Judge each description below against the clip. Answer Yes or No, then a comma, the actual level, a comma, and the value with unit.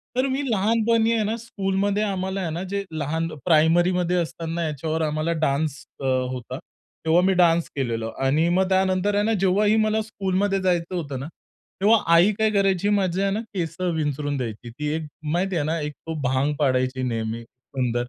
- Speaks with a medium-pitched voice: Yes, medium, 170 Hz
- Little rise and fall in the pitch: No, average, 5.2 semitones